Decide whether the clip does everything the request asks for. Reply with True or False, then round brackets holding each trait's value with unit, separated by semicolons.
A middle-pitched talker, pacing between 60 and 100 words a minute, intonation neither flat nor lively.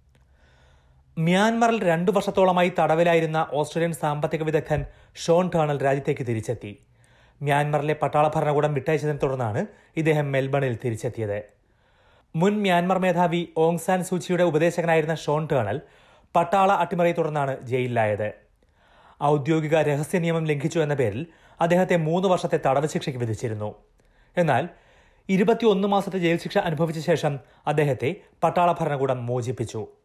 False (155 Hz; 110 wpm; 4.6 semitones)